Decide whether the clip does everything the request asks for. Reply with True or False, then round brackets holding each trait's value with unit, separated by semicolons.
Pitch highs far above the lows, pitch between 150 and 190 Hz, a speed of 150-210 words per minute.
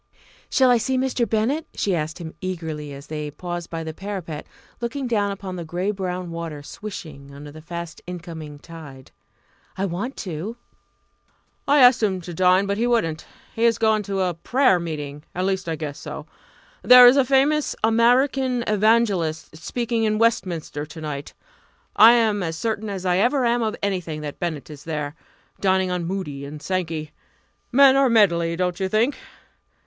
True (6.0 semitones; 185 Hz; 175 wpm)